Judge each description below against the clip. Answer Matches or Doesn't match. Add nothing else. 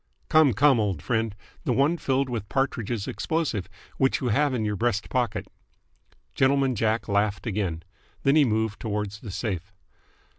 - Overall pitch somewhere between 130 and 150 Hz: Doesn't match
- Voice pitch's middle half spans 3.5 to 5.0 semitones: Matches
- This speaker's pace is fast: Doesn't match